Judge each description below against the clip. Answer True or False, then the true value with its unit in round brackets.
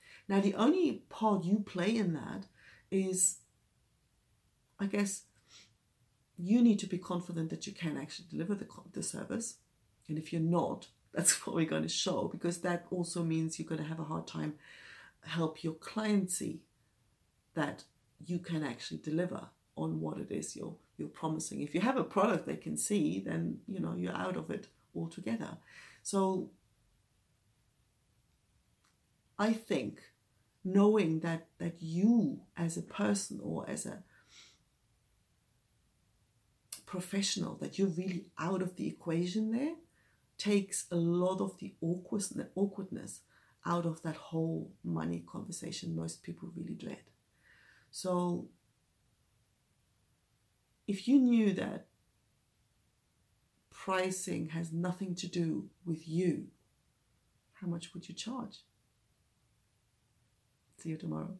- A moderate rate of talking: False (130 wpm)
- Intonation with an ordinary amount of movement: False (8.6 semitones)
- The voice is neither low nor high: True (165 Hz)